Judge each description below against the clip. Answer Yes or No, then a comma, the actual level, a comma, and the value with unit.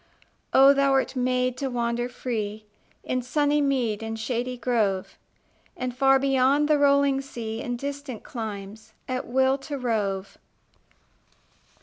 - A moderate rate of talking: No, slow, 130 wpm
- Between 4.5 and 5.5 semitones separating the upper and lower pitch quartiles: No, average, 3.4 semitones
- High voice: Yes, very high, 255 Hz